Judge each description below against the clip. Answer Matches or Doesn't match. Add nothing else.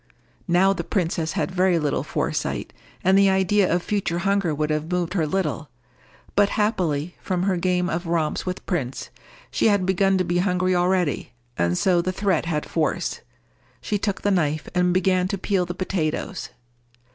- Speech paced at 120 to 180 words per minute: Matches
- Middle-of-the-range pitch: Matches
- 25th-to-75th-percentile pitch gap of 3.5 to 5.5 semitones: Doesn't match